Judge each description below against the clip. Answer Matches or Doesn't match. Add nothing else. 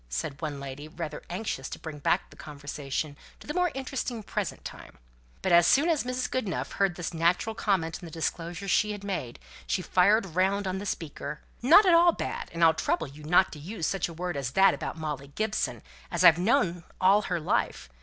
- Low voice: Doesn't match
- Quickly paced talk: Matches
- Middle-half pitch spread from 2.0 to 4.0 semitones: Doesn't match